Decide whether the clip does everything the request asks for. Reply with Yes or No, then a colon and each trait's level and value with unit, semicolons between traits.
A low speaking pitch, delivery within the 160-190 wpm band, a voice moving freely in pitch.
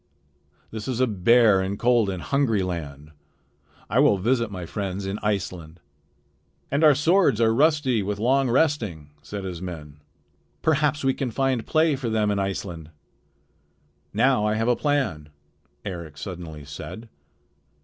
No: low, 105 Hz; average, 150 wpm; wide, 6.2 semitones